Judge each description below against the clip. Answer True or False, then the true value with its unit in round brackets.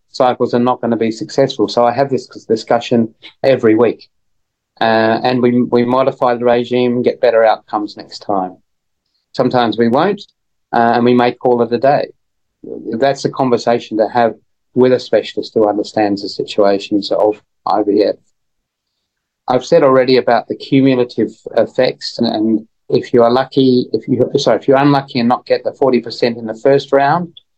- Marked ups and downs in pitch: False (2.7 semitones)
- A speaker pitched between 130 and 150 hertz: False (120 Hz)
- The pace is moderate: True (175 wpm)